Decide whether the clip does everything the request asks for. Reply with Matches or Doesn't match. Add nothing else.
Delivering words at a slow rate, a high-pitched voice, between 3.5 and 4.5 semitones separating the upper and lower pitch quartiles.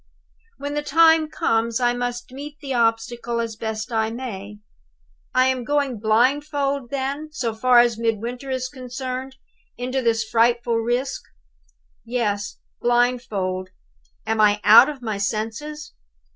Doesn't match